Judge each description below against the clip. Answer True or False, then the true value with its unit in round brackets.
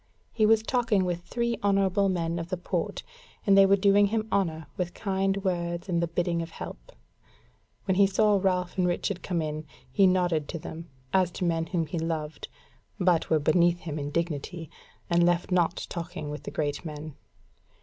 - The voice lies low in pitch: False (175 Hz)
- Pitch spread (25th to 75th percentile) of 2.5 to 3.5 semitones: True (2.9 semitones)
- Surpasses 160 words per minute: True (190 wpm)